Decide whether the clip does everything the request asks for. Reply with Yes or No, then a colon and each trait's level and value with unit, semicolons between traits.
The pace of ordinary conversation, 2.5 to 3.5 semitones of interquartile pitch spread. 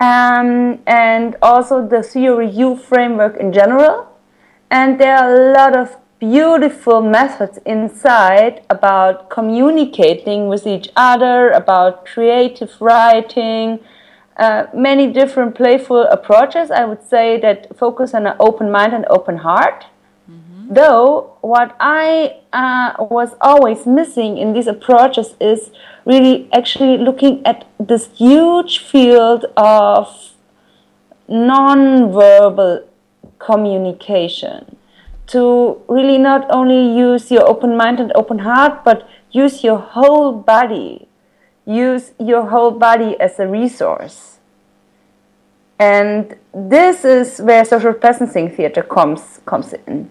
No: slow, 115 wpm; average, 3.2 semitones